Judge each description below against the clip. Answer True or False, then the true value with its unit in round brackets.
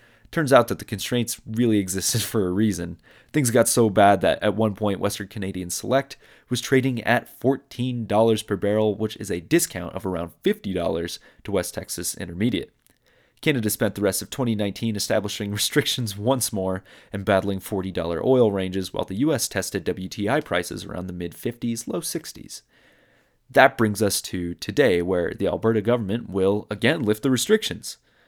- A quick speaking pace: False (170 wpm)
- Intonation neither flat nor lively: True (3.8 semitones)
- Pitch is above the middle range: False (105 Hz)